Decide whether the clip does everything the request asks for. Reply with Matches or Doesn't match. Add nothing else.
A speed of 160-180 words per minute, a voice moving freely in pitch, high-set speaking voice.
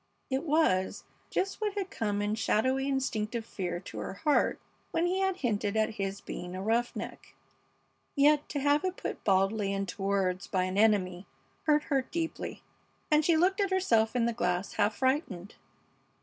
Matches